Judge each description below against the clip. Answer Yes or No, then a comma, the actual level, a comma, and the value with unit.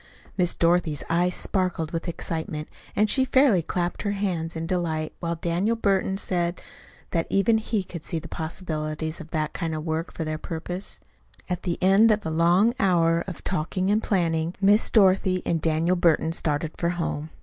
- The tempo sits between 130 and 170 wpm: No, average, 180 wpm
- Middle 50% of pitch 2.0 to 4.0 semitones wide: Yes, average, 2.9 semitones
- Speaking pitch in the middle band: Yes, medium, 170 Hz